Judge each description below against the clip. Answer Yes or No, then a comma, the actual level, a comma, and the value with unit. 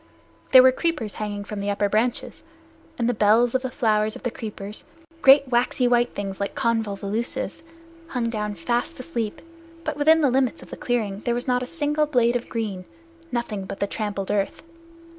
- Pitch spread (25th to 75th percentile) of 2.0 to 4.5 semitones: Yes, average, 3.4 semitones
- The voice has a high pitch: Yes, high, 235 Hz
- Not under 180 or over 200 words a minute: Yes, average, 185 wpm